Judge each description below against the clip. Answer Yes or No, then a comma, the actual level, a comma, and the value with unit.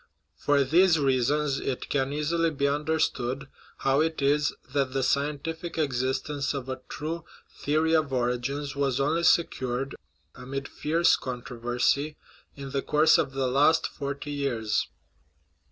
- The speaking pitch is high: No, medium, 140 Hz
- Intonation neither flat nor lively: No, narrow, 2.3 semitones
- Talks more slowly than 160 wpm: Yes, average, 140 wpm